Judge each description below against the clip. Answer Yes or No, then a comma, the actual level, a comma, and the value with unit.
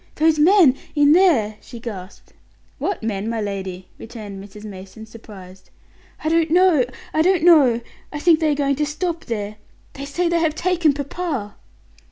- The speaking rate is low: No, average, 170 wpm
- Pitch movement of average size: No, wide, 7.5 semitones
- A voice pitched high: Yes, very high, 280 Hz